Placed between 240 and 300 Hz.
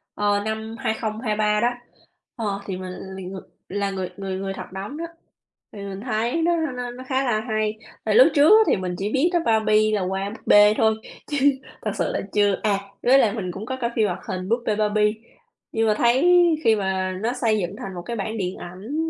No: high, 215 Hz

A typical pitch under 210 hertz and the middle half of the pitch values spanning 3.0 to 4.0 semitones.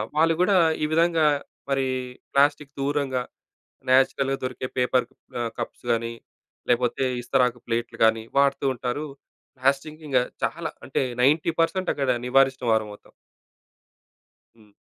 Yes: low, 135 Hz; average, 3.4 semitones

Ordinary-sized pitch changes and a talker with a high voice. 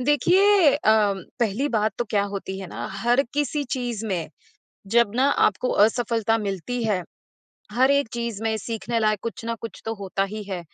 Yes: average, 3.2 semitones; high, 225 Hz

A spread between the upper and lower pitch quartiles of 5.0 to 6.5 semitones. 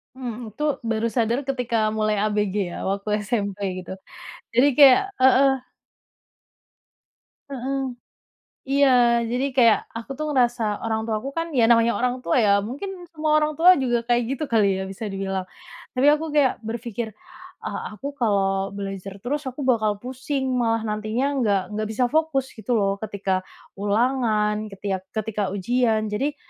No: average, 3.9 semitones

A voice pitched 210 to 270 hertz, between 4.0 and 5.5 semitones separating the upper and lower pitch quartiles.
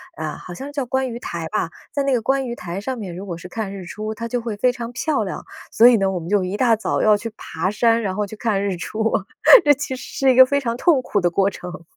Yes: high, 220 Hz; average, 4.5 semitones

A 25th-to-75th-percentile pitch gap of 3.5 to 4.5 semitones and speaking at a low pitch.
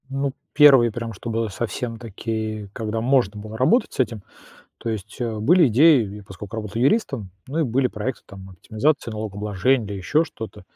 Yes: average, 3.8 semitones; low, 115 Hz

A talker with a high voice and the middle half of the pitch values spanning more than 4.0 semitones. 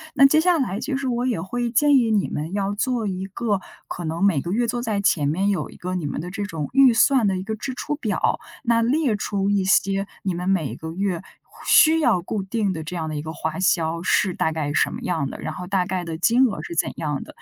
Yes: high, 195 Hz; wide, 5.5 semitones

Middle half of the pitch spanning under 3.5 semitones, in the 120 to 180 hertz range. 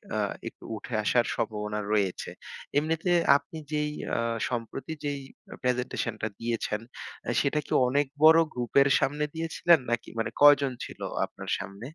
No: average, 4.7 semitones; low, 130 Hz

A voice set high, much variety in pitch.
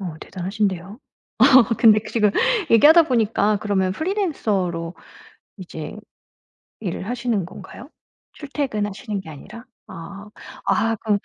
No: high, 210 Hz; average, 3.7 semitones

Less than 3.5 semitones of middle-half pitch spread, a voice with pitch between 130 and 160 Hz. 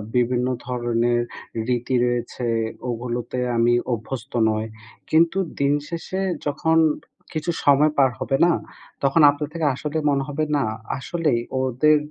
No: average, 4.0 semitones; low, 135 Hz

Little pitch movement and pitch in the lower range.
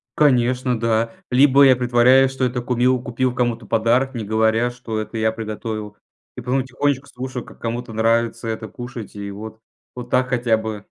Yes: narrow, 2.3 semitones; low, 120 Hz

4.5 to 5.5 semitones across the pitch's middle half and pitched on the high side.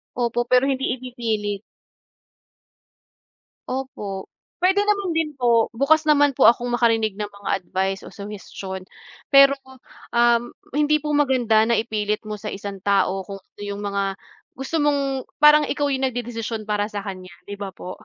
Yes: average, 5.0 semitones; high, 235 Hz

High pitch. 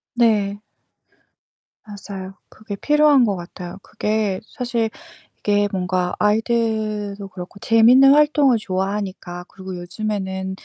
Yes: high, 205 Hz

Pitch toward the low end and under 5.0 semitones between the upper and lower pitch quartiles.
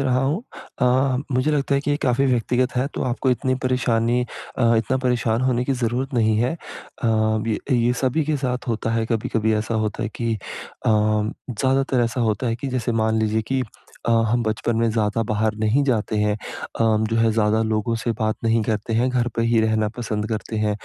Yes: low, 115 Hz; narrow, 2.5 semitones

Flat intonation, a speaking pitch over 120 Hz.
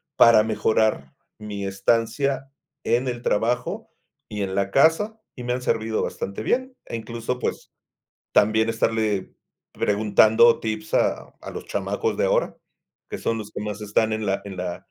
No: narrow, 2.3 semitones; low, 110 Hz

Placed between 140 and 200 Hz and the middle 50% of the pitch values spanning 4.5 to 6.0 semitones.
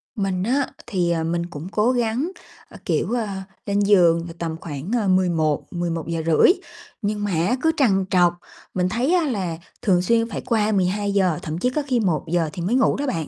Yes: high, 190 Hz; average, 4.9 semitones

